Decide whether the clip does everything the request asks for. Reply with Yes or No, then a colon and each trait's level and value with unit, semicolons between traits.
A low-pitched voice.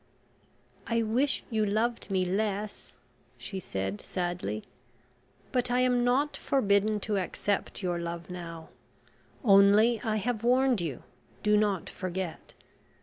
No: high, 205 Hz